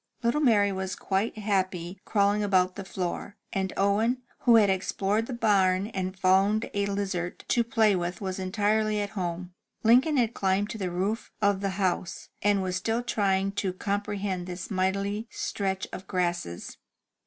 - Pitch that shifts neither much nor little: No, narrow, 2.2 semitones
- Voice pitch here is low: No, high, 195 Hz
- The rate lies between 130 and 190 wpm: Yes, average, 165 wpm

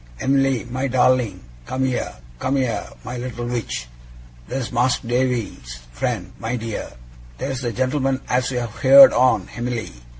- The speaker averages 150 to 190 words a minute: No, average, 140 wpm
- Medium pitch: No, low, 125 Hz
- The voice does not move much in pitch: Yes, narrow, 2.0 semitones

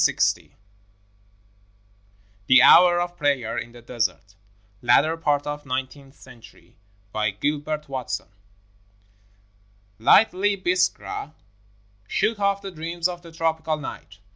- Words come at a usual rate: No, slow, 110 wpm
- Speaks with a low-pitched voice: No, medium, 150 Hz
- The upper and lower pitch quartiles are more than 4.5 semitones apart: Yes, average, 5.2 semitones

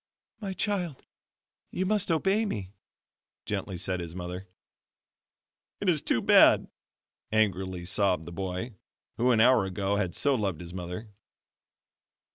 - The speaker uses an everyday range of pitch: No, wide, 7.7 semitones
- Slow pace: Yes, slow, 130 wpm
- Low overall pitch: Yes, low, 100 Hz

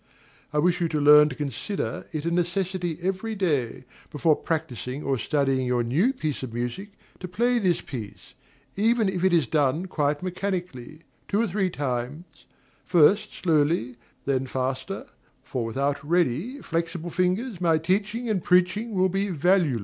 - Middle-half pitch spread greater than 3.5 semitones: Yes, average, 5.1 semitones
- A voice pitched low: No, medium, 165 Hz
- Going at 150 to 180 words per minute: Yes, average, 155 wpm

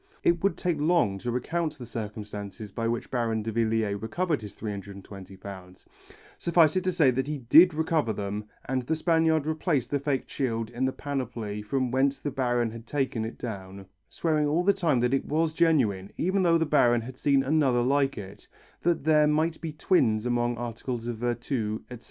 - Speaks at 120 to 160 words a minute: No, average, 185 wpm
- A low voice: Yes, low, 125 Hz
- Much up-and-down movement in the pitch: Yes, wide, 5.7 semitones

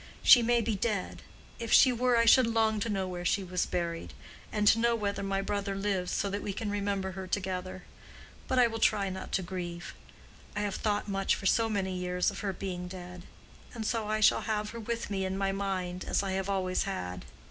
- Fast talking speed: Yes, fast, 220 wpm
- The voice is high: Yes, high, 195 Hz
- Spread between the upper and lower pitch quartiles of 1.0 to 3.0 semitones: Yes, average, 2.7 semitones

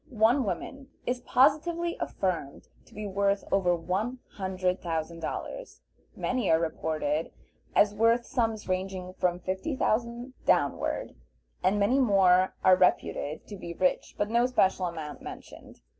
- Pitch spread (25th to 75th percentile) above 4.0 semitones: Yes, average, 4.7 semitones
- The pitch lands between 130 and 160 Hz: No, high, 195 Hz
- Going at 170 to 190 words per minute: No, average, 140 wpm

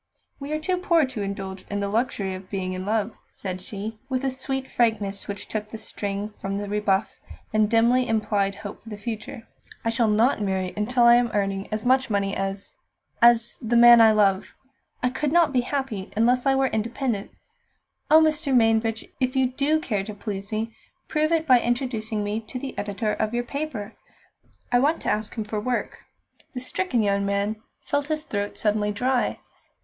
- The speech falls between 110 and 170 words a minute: No, average, 195 wpm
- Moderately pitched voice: No, high, 225 Hz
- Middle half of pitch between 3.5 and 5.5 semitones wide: Yes, average, 3.9 semitones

